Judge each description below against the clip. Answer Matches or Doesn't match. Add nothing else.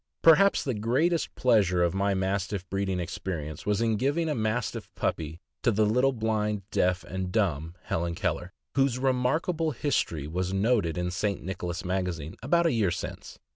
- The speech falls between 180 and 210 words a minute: Doesn't match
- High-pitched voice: Doesn't match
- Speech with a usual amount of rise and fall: Doesn't match